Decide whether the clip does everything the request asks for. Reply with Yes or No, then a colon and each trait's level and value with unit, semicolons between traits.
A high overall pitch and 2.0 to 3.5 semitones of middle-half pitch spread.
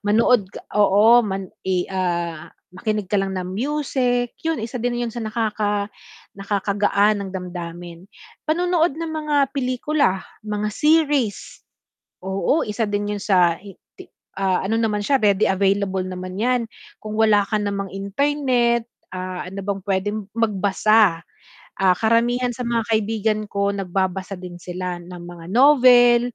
No: high, 205 Hz; average, 4.0 semitones